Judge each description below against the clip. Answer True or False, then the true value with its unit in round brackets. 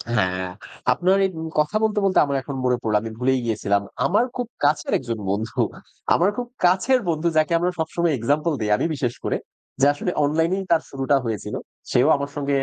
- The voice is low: False (145 Hz)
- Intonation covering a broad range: True (6.1 semitones)